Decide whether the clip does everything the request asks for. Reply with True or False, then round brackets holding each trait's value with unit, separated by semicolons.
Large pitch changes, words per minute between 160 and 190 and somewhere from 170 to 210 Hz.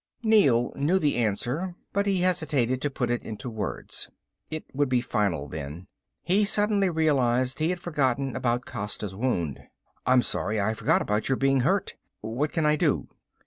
False (5.8 semitones; 170 wpm; 130 Hz)